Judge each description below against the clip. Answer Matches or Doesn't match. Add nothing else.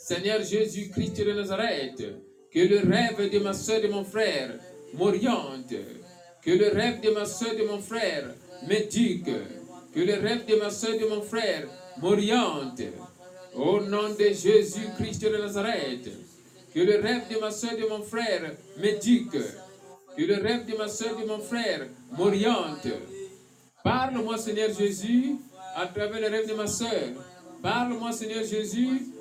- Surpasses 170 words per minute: Doesn't match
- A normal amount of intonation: Doesn't match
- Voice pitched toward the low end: Doesn't match